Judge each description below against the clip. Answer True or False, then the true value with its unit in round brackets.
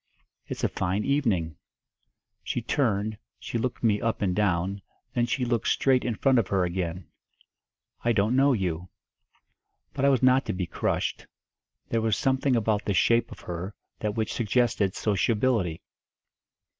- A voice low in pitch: True (110 Hz)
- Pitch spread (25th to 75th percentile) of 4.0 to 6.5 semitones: True (4.5 semitones)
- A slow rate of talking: False (155 wpm)